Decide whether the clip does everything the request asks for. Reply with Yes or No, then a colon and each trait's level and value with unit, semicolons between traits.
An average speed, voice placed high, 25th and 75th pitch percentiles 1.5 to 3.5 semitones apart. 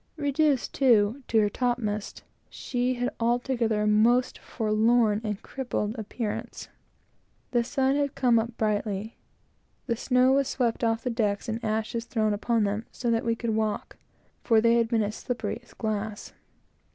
Yes: average, 165 wpm; high, 230 Hz; narrow, 2.4 semitones